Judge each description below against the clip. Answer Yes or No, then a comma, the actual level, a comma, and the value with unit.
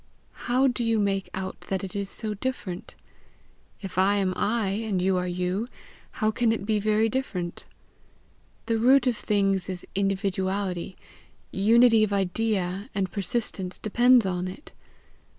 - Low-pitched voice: No, high, 200 Hz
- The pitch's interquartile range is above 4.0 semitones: No, average, 3.0 semitones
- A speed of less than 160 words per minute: Yes, average, 150 wpm